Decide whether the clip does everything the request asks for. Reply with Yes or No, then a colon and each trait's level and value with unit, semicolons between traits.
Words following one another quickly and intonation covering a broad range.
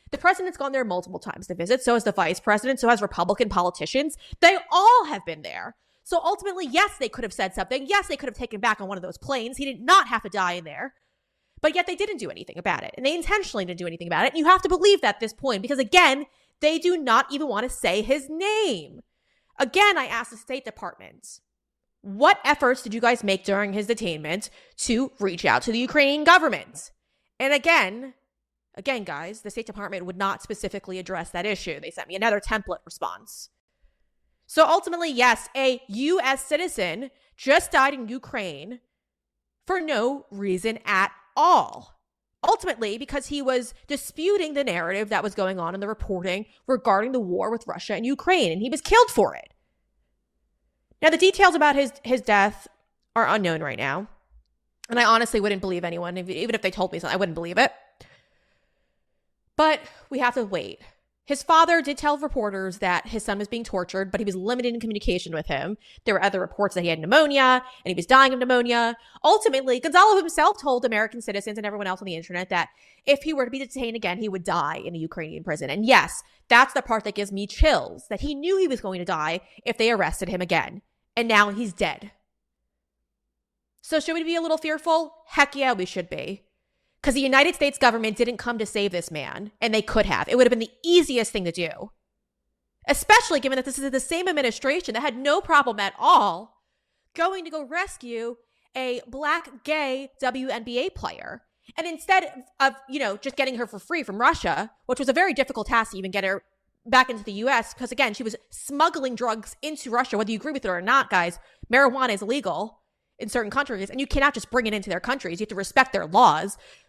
Yes: fast, 210 wpm; wide, 6.2 semitones